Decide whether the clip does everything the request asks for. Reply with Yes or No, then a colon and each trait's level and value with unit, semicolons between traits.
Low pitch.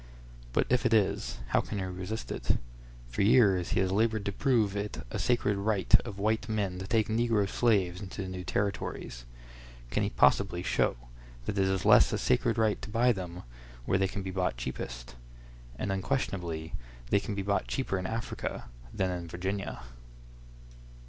Yes: low, 100 Hz